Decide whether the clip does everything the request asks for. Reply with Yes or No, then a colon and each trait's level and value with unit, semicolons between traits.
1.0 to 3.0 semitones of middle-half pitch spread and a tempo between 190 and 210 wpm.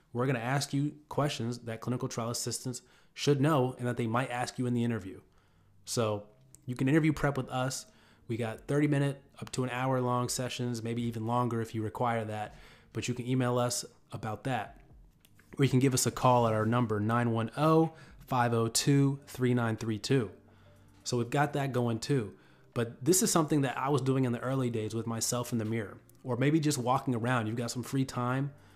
Yes: average, 2.7 semitones; fast, 205 wpm